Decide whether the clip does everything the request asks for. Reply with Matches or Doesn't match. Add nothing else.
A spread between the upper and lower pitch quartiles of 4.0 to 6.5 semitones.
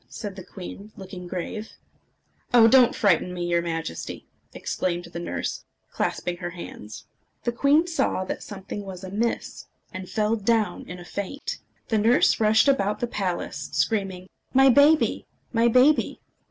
Matches